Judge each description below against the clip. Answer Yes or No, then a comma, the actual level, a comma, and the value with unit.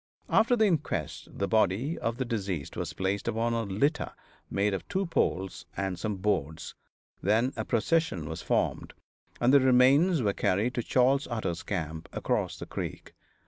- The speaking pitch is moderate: No, low, 110 Hz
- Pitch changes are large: Yes, wide, 5.7 semitones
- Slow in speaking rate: No, average, 165 wpm